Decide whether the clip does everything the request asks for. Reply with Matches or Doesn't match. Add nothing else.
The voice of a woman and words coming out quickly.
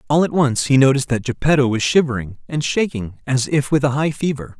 Doesn't match